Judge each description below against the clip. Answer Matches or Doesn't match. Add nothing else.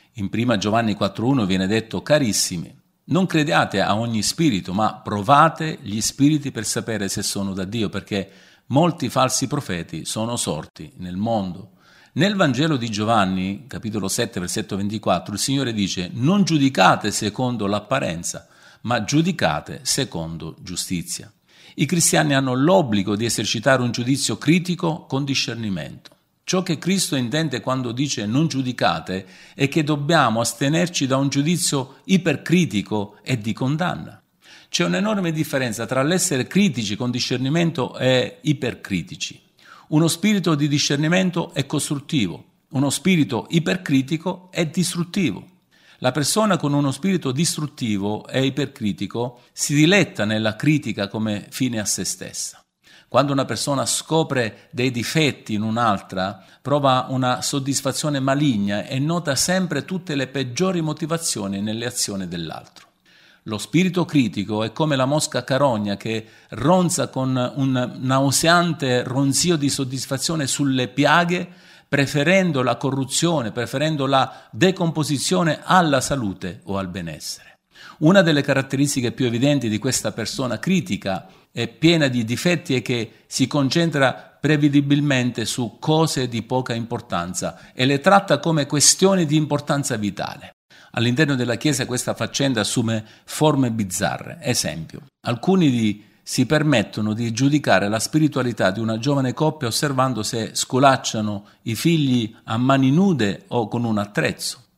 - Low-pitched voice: Matches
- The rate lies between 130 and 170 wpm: Matches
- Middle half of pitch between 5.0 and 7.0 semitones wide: Matches